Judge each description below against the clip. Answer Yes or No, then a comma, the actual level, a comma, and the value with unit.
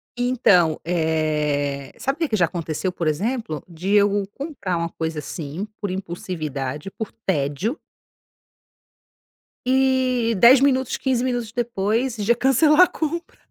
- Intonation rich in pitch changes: Yes, wide, 7.9 semitones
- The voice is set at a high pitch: Yes, high, 200 Hz